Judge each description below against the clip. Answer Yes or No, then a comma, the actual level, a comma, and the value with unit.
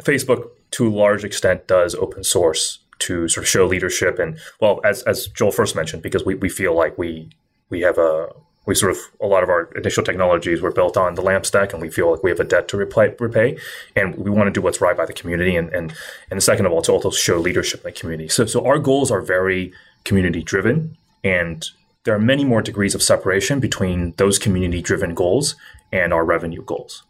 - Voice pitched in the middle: No, low, 110 Hz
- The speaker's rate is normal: No, fast, 230 wpm